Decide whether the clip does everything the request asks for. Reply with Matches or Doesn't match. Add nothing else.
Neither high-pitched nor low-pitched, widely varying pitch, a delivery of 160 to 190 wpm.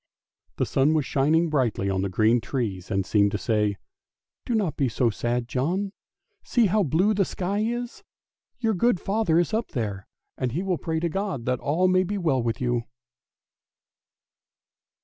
Matches